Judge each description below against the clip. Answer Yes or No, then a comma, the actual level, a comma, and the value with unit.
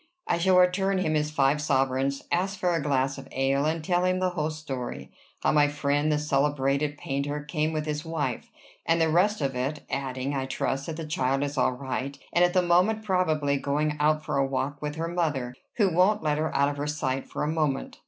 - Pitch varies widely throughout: No, average, 3.1 semitones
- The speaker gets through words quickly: Yes, fast, 220 wpm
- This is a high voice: No, medium, 150 Hz